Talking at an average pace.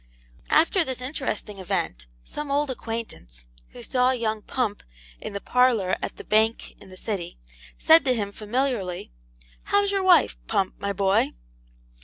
Yes: average, 150 wpm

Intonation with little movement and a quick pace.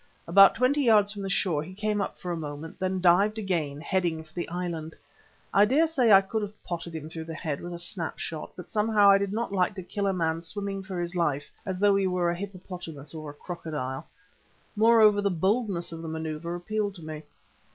No: average, 3.8 semitones; fast, 225 wpm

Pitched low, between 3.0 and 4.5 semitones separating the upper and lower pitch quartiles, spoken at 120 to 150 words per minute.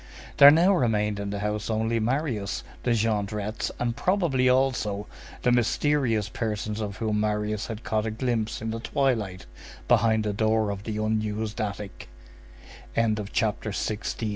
No: low, 110 Hz; narrow, 2.4 semitones; average, 140 wpm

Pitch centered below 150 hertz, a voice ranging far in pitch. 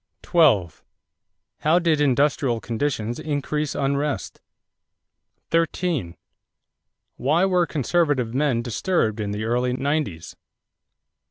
No: medium, 140 Hz; average, 4.9 semitones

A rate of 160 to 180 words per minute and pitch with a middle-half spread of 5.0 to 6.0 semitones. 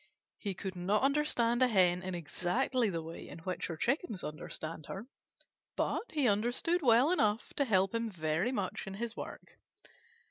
Yes: average, 170 wpm; wide, 5.5 semitones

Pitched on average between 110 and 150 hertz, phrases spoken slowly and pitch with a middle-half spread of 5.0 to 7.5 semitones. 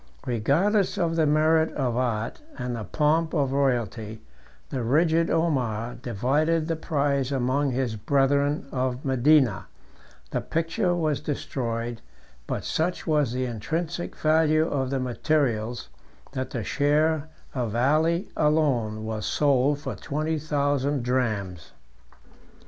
No: medium, 140 Hz; slow, 125 wpm; average, 4.3 semitones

